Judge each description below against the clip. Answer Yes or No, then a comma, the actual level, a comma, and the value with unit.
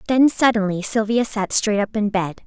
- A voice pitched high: Yes, high, 215 Hz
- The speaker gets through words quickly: No, average, 195 wpm